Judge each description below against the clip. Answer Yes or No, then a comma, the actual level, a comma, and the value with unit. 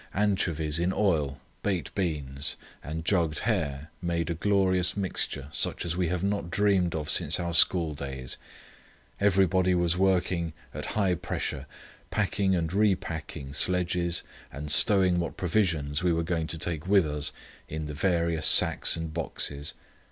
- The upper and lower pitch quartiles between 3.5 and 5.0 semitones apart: No, average, 3.1 semitones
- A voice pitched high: No, very low, 85 Hz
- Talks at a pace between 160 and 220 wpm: No, average, 150 wpm